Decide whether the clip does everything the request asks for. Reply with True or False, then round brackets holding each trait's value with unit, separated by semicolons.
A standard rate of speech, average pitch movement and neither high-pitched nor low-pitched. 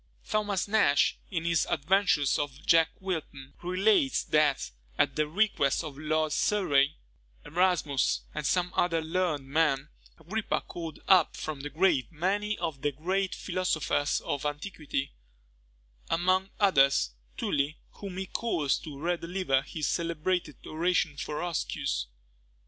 False (130 wpm; 4.1 semitones; 165 Hz)